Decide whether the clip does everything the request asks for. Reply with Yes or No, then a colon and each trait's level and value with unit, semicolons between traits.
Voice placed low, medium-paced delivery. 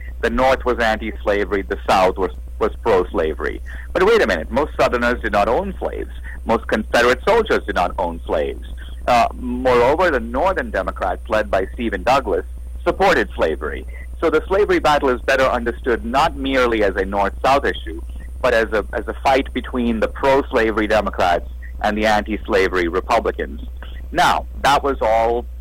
Yes: low, 100 Hz; average, 170 wpm